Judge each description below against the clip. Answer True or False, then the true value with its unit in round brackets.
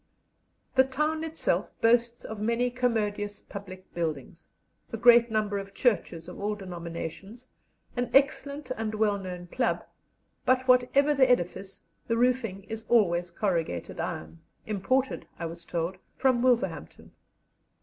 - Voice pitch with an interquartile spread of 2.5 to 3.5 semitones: False (5.1 semitones)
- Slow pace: True (130 wpm)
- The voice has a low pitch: False (220 Hz)